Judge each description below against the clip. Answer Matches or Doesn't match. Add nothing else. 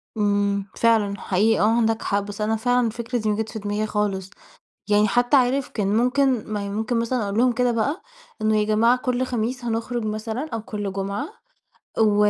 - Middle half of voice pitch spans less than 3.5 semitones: Matches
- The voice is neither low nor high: Doesn't match